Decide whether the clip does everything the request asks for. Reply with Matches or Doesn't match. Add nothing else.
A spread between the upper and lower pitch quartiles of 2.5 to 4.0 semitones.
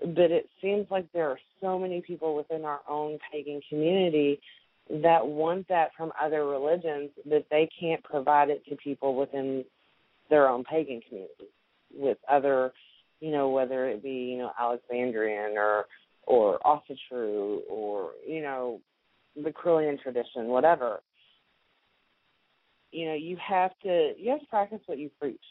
Doesn't match